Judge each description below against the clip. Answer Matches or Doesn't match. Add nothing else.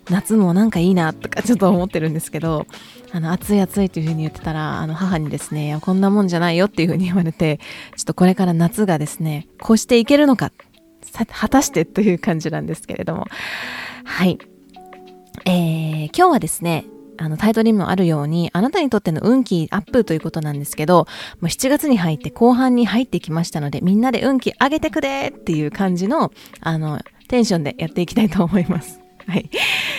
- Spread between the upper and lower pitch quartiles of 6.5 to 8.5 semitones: Doesn't match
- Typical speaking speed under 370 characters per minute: Doesn't match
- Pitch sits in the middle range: Matches